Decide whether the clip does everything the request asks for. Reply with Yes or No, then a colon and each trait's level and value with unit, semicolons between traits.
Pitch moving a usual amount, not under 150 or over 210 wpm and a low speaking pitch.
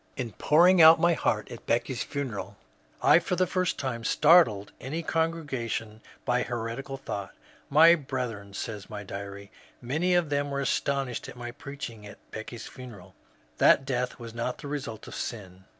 Yes: average, 4.7 semitones; average, 180 wpm; low, 125 Hz